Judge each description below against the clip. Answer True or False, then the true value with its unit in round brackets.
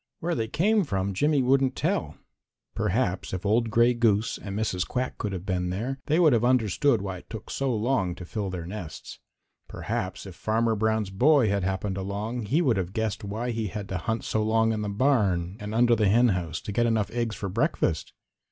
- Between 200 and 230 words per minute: True (205 wpm)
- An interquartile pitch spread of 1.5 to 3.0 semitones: False (3.7 semitones)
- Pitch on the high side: False (110 Hz)